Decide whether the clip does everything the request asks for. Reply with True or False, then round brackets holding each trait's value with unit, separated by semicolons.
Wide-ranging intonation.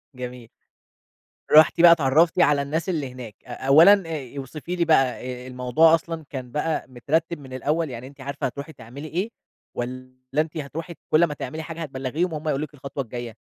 False (4.0 semitones)